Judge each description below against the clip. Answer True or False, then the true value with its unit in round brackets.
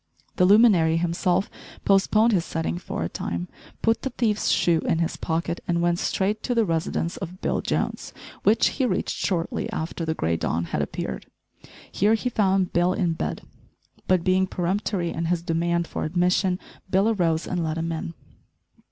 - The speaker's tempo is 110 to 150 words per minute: False (175 wpm)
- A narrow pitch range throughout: False (3.0 semitones)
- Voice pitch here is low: False (175 Hz)